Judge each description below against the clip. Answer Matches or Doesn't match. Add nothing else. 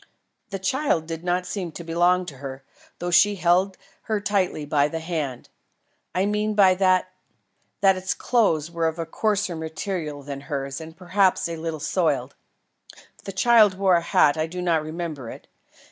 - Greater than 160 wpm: Matches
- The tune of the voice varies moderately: Matches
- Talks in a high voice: Doesn't match